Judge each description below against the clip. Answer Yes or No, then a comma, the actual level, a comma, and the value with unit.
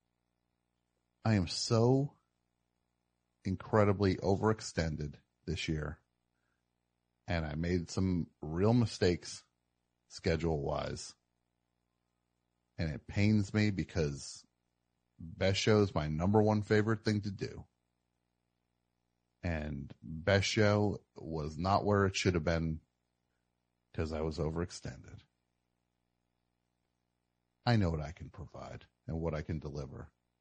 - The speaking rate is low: Yes, slow, 110 wpm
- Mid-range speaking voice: No, very low, 75 Hz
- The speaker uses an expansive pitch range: Yes, wide, 7.8 semitones